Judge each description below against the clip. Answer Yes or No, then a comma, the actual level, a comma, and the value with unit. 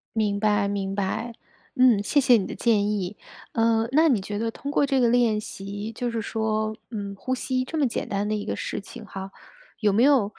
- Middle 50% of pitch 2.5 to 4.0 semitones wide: Yes, average, 3.1 semitones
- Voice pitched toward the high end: Yes, high, 220 Hz